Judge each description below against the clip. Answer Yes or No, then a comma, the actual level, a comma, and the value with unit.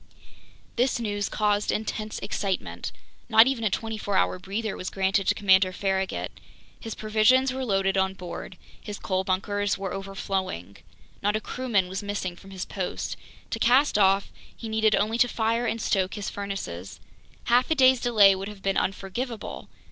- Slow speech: No, average, 165 wpm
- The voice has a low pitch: No, high, 205 Hz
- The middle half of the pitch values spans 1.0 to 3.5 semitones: Yes, average, 2.7 semitones